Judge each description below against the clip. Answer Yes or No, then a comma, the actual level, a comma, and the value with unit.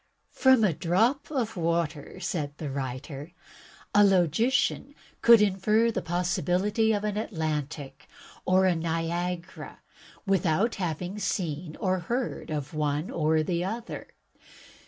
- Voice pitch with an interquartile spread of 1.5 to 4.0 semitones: No, average, 4.8 semitones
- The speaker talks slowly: Yes, slow, 120 wpm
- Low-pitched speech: No, medium, 180 Hz